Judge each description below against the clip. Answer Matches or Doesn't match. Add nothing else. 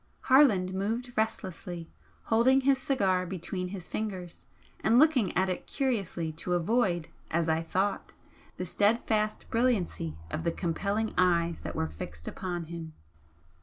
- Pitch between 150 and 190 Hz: Matches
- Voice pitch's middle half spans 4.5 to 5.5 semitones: Matches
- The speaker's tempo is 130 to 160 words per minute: Matches